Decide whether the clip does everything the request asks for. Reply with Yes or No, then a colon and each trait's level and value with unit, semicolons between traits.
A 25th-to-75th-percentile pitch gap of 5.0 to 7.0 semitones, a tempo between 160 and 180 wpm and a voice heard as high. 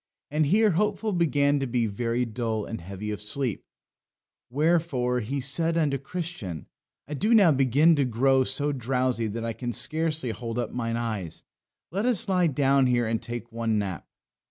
No: average, 5.3 semitones; average, 175 wpm; low, 130 Hz